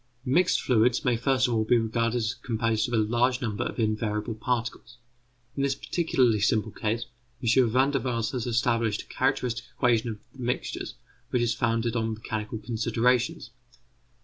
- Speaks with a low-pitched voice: Yes, low, 115 Hz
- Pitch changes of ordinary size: No, narrow, 2.0 semitones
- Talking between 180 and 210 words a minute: No, average, 170 wpm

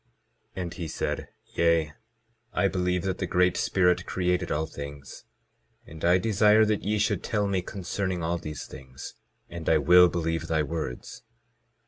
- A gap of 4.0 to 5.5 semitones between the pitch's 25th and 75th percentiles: No, average, 2.7 semitones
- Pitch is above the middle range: No, very low, 90 Hz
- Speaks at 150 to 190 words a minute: Yes, average, 160 wpm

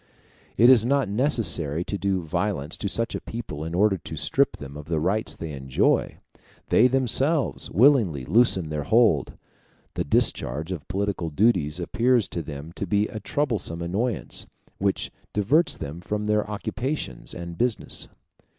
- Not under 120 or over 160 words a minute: Yes, average, 155 wpm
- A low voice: Yes, low, 100 Hz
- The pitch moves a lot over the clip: Yes, wide, 6.4 semitones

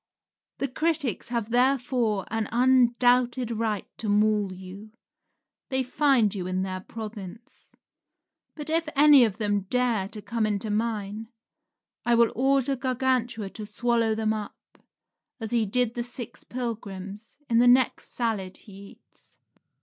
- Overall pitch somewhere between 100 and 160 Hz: No, high, 230 Hz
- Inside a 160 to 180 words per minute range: No, average, 140 wpm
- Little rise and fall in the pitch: No, average, 3.1 semitones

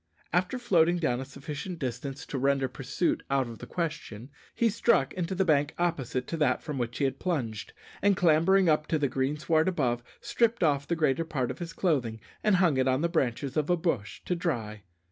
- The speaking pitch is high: No, medium, 150 Hz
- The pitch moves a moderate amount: Yes, average, 4.8 semitones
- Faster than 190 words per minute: Yes, fast, 205 wpm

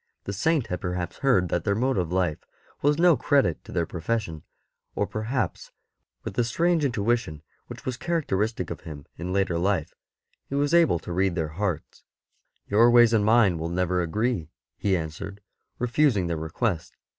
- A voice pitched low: Yes, low, 100 Hz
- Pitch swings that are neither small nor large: No, wide, 5.9 semitones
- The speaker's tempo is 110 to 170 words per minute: No, average, 180 wpm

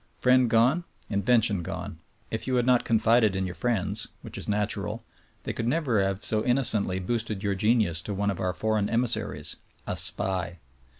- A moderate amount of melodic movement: Yes, average, 3.5 semitones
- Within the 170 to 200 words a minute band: Yes, average, 180 wpm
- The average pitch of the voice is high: No, low, 110 Hz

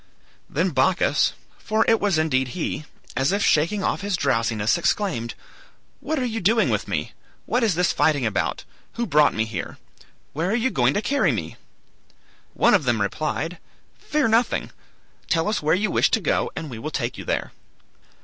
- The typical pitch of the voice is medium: Yes, medium, 170 Hz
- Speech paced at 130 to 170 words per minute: No, average, 180 wpm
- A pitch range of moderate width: No, wide, 8.2 semitones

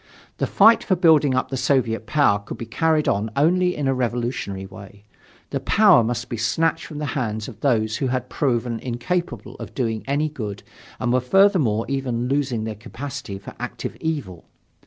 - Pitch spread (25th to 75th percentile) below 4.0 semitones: No, average, 4.6 semitones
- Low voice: Yes, low, 125 Hz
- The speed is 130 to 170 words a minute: No, average, 180 wpm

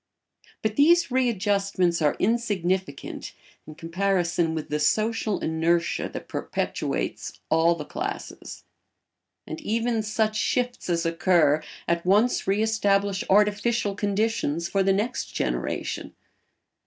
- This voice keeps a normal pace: No, slow, 115 wpm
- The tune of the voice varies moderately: Yes, average, 4.6 semitones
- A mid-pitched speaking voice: No, high, 200 Hz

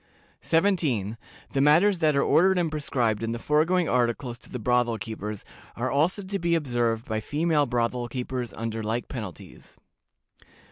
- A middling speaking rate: Yes, average, 155 wpm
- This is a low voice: Yes, low, 125 Hz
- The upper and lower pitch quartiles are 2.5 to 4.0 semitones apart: No, wide, 5.5 semitones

